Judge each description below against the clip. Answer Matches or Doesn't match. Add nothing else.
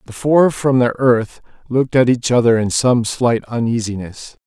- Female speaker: Doesn't match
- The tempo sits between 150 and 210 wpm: Matches